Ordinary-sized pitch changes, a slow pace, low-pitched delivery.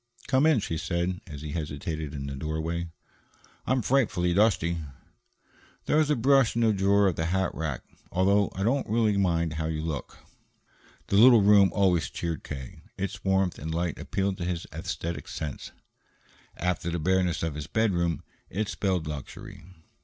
No: average, 3.9 semitones; average, 170 wpm; very low, 90 Hz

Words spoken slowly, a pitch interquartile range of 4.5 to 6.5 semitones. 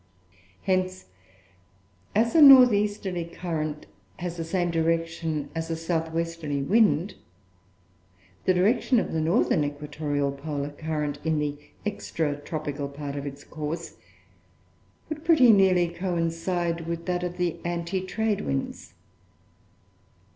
No: slow, 125 wpm; average, 3.6 semitones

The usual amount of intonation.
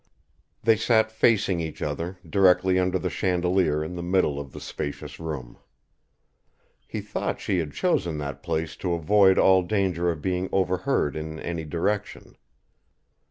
Yes: average, 3.2 semitones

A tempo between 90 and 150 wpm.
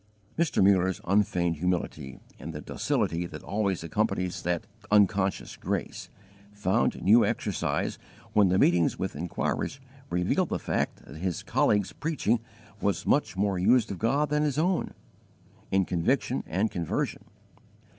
Yes: slow, 135 wpm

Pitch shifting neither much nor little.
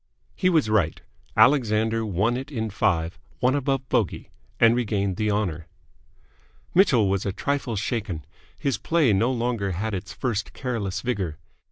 Yes: average, 4.3 semitones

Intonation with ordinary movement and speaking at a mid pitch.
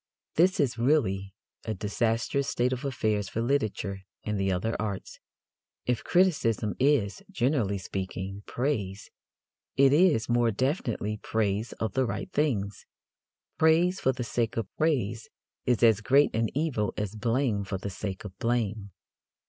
No: average, 4.6 semitones; low, 115 Hz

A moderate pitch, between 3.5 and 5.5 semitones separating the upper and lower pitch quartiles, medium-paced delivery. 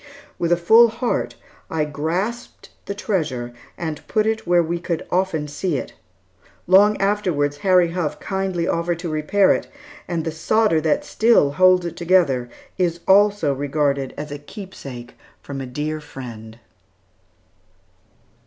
Yes: medium, 170 Hz; average, 4.6 semitones; average, 145 wpm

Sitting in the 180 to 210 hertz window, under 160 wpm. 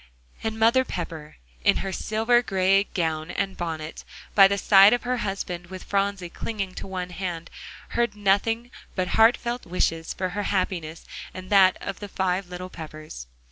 No: high, 190 Hz; average, 170 wpm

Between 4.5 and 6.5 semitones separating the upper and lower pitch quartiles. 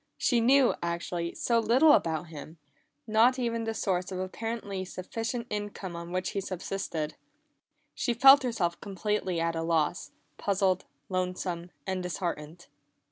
Yes: average, 4.8 semitones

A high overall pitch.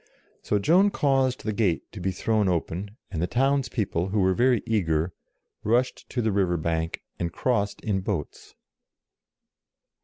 No: low, 100 Hz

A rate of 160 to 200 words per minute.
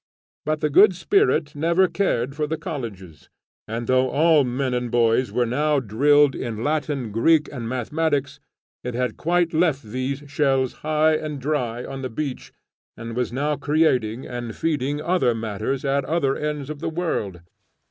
Yes: average, 165 wpm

